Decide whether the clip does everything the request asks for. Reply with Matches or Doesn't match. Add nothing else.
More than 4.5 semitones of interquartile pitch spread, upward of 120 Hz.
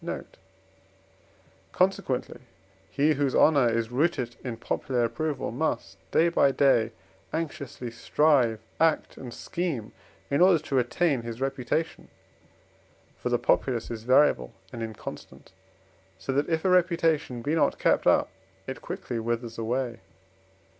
Matches